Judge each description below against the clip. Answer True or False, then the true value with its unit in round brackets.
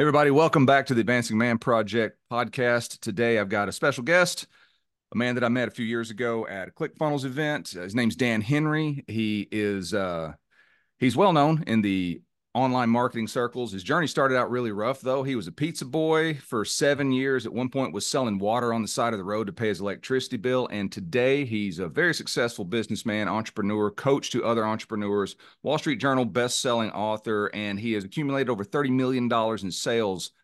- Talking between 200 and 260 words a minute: True (205 wpm)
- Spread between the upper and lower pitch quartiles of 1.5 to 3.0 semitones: False (3.8 semitones)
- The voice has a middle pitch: False (120 Hz)